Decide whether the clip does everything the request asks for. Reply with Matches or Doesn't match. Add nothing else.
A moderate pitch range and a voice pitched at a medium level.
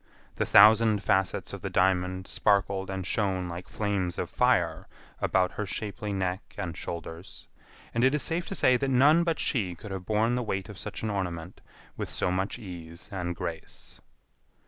Doesn't match